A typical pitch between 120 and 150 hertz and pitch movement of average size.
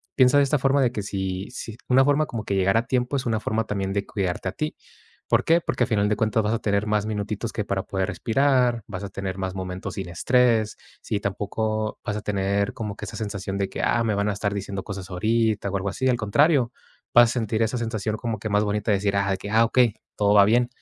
No: low, 105 Hz; average, 3.0 semitones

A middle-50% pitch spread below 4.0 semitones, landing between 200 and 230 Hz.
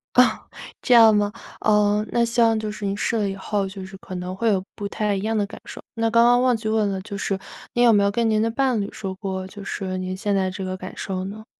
Yes: narrow, 2.6 semitones; high, 205 Hz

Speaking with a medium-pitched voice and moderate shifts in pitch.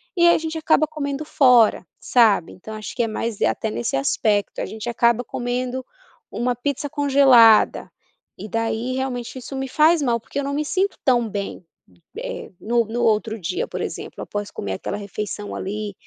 No: high, 240 Hz; average, 4.3 semitones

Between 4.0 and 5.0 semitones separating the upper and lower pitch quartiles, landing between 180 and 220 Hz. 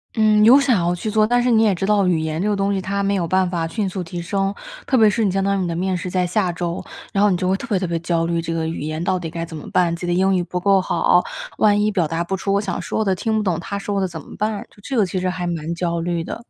No: average, 2.9 semitones; medium, 185 Hz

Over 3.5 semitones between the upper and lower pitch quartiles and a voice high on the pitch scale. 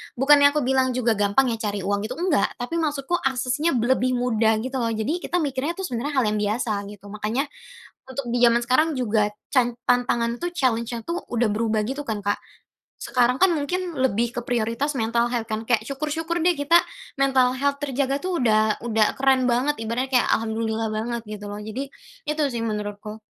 Yes: average, 3.9 semitones; high, 245 Hz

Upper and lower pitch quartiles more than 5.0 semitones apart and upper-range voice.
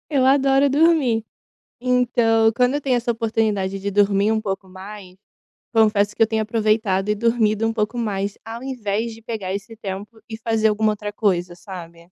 No: narrow, 2.4 semitones; high, 220 Hz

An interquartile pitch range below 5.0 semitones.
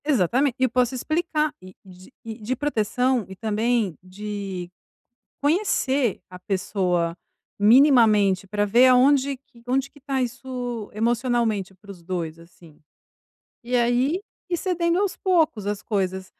No: wide, 5.4 semitones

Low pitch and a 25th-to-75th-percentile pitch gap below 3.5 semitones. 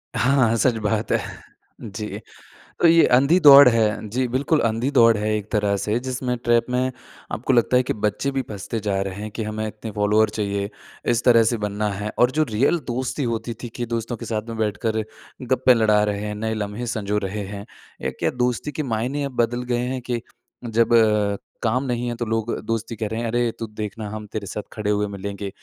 Yes: low, 115 Hz; average, 2.7 semitones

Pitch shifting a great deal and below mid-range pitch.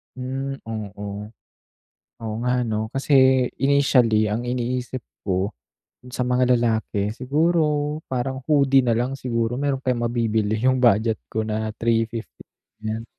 No: average, 2.9 semitones; low, 120 Hz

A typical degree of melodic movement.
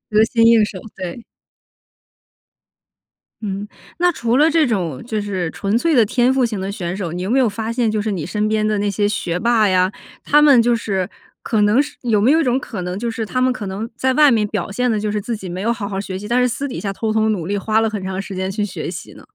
Yes: average, 3.4 semitones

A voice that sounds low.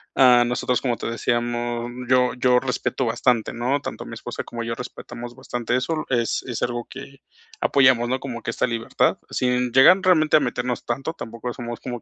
Yes: low, 125 Hz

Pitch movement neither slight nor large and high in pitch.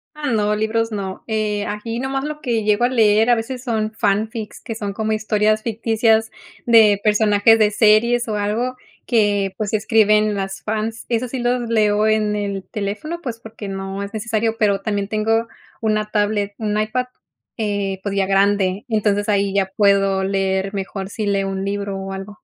No: narrow, 1.9 semitones; high, 215 Hz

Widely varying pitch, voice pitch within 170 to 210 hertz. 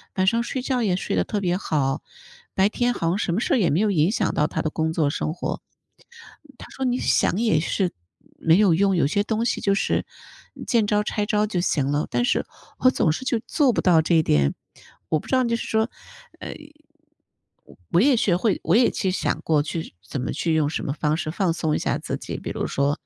Yes: wide, 6.4 semitones; high, 190 Hz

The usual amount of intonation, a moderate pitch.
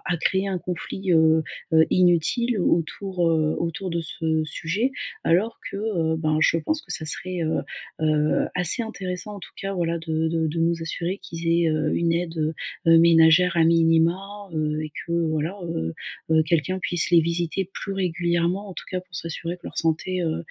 No: narrow, 2.3 semitones; medium, 170 Hz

